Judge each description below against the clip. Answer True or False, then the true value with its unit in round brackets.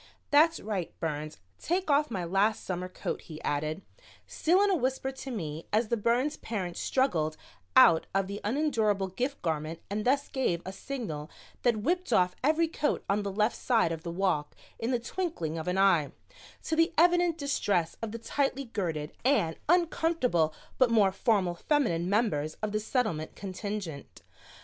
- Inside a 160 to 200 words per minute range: True (170 wpm)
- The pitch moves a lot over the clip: True (7.8 semitones)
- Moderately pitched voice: False (210 Hz)